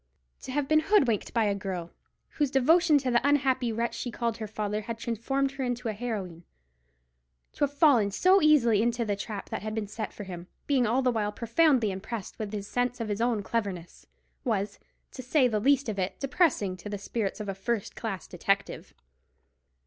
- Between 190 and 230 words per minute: Yes, average, 195 wpm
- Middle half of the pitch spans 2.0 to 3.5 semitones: No, average, 4.3 semitones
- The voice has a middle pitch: No, high, 225 Hz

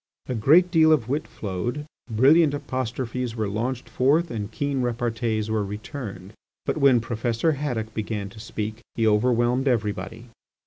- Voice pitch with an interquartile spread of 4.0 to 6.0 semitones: No, average, 3.6 semitones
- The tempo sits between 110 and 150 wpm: Yes, average, 145 wpm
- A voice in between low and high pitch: No, low, 120 Hz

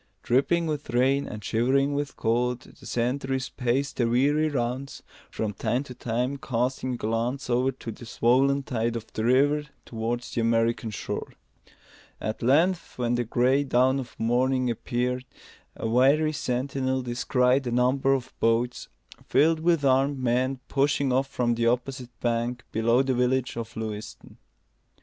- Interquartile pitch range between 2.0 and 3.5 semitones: Yes, narrow, 2.4 semitones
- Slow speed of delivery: No, average, 150 wpm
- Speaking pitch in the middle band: No, low, 125 Hz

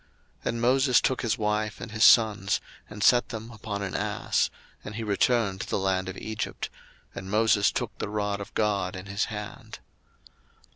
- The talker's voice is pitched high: No, low, 105 Hz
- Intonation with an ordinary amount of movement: No, narrow, 2.1 semitones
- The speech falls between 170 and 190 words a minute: Yes, average, 185 wpm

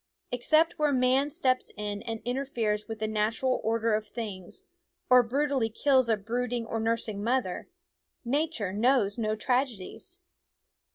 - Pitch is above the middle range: Yes, high, 230 Hz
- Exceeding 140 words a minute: No, slow, 135 wpm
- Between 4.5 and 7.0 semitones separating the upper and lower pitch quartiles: No, average, 3.4 semitones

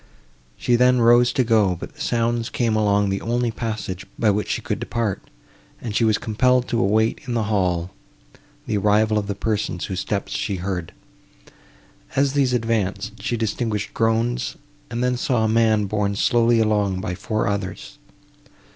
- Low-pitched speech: Yes, low, 110 Hz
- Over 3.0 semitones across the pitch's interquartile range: No, average, 2.7 semitones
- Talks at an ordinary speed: Yes, average, 170 wpm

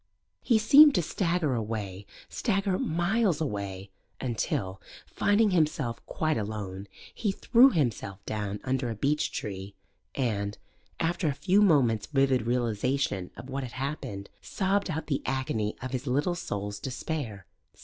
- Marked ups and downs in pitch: Yes, wide, 8.0 semitones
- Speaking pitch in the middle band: No, low, 130 Hz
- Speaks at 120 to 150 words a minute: Yes, average, 140 wpm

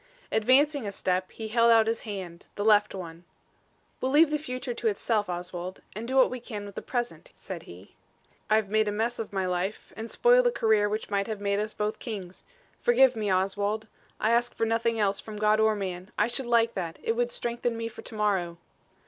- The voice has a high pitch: Yes, high, 215 Hz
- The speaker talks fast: Yes, fast, 215 wpm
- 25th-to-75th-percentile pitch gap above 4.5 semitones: No, average, 2.8 semitones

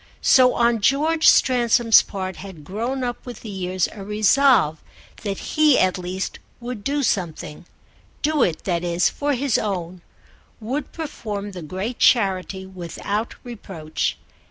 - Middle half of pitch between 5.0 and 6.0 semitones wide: Yes, average, 5.3 semitones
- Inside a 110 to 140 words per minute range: Yes, slow, 135 wpm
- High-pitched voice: Yes, high, 210 Hz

